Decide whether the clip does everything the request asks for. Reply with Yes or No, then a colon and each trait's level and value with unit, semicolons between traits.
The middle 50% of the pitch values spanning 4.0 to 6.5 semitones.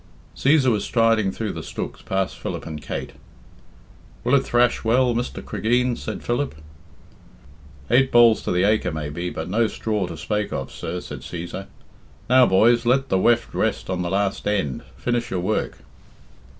Yes: average, 4.3 semitones